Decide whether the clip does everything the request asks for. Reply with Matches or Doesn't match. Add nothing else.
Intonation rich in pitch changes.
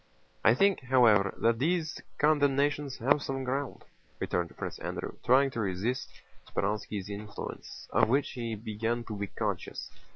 Doesn't match